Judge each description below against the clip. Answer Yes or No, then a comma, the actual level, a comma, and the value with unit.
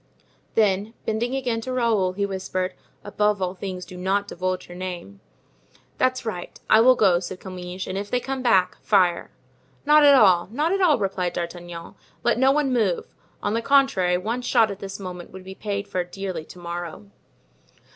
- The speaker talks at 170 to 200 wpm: Yes, average, 180 wpm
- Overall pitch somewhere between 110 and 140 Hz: No, high, 195 Hz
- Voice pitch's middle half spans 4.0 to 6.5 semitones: Yes, average, 4.3 semitones